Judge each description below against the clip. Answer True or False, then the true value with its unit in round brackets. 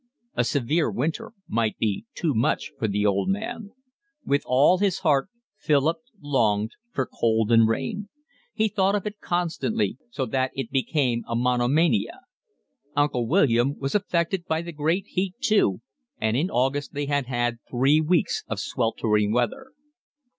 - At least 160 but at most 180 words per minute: False (150 wpm)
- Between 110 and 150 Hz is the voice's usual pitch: True (140 Hz)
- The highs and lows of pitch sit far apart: True (6.7 semitones)